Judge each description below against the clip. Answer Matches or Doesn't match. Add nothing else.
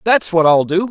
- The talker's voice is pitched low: Doesn't match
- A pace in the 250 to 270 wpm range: Matches